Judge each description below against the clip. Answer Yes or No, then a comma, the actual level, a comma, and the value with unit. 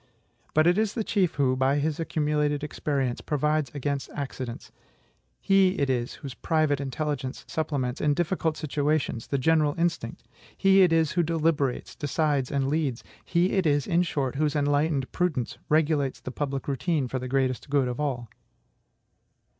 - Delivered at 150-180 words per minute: Yes, average, 160 wpm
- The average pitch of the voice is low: No, medium, 145 Hz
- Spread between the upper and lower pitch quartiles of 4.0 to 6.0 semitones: No, average, 3.1 semitones